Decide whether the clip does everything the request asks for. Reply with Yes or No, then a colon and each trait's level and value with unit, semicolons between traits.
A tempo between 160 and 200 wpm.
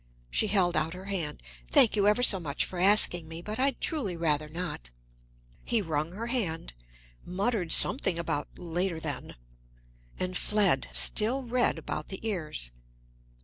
No: average, 150 wpm